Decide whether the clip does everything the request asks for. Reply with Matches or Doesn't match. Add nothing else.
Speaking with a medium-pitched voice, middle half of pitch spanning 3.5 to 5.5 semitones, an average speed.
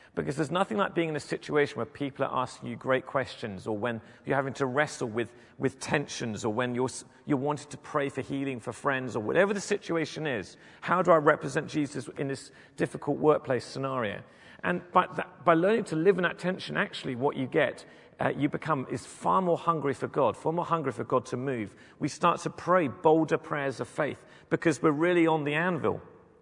Doesn't match